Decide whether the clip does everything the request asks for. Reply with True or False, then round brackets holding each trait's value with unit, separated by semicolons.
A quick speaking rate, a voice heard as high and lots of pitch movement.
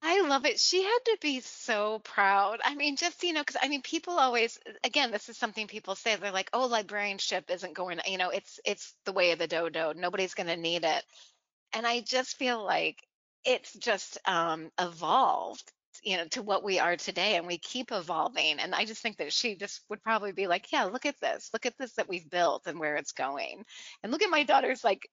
True (230 wpm; 215 Hz; 5.9 semitones)